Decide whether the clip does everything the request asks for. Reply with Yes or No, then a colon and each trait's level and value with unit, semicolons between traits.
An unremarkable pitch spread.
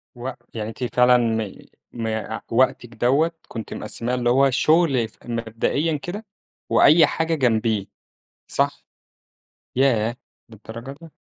Yes: average, 3.7 semitones